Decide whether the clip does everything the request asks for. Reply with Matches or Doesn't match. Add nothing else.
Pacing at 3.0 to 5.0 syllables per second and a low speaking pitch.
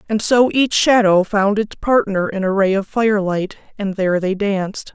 Doesn't match